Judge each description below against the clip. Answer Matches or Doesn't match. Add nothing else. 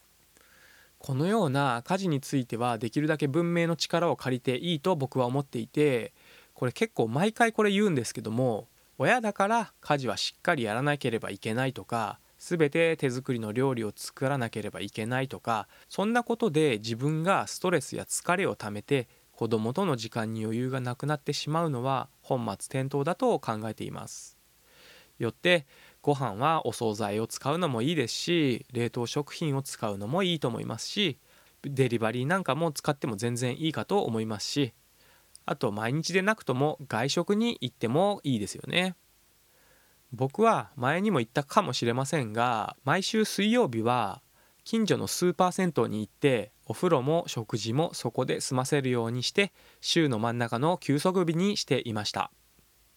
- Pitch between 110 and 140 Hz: Matches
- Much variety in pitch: Matches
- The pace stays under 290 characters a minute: Doesn't match